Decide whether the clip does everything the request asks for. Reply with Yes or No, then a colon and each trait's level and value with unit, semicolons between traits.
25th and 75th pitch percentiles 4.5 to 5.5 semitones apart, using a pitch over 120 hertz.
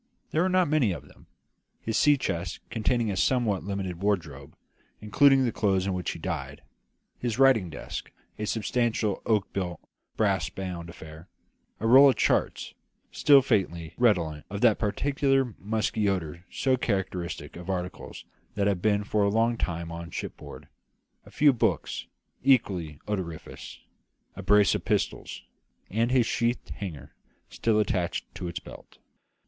No: average, 5.0 semitones; low, 100 Hz